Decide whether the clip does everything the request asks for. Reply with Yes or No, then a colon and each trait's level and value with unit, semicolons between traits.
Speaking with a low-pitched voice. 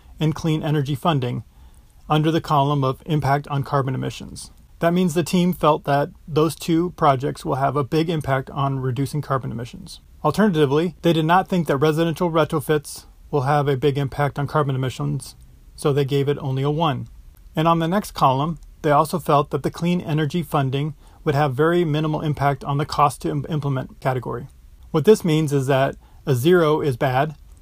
No: medium, 150 Hz